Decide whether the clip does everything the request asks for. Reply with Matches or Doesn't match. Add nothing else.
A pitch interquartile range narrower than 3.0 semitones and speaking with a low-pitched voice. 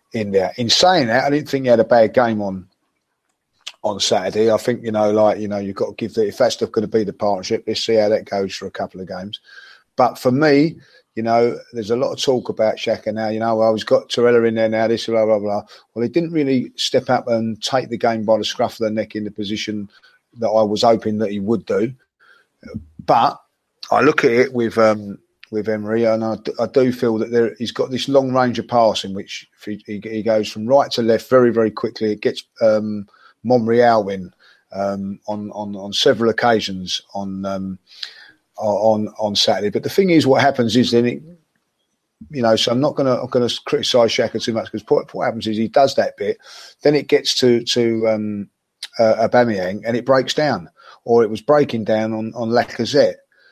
Matches